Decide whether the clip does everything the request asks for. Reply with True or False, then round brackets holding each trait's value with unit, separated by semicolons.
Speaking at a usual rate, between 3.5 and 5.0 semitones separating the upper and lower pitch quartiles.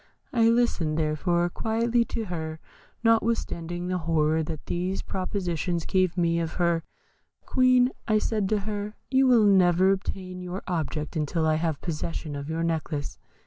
True (150 wpm; 4.4 semitones)